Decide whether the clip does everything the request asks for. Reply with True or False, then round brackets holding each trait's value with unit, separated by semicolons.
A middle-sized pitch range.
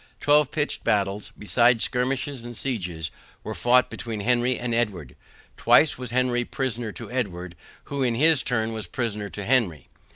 True (3.5 semitones)